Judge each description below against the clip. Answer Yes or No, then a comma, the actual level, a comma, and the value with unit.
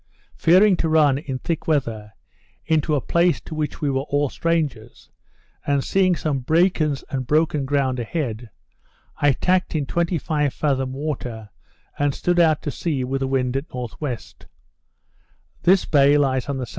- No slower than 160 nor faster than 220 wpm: Yes, average, 170 wpm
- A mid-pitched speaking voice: Yes, medium, 145 Hz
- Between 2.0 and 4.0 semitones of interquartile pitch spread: Yes, average, 3.4 semitones